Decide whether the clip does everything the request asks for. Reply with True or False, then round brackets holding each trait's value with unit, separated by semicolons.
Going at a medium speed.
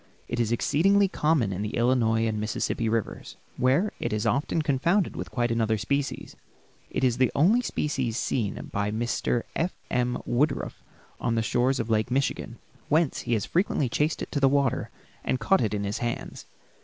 True (180 wpm)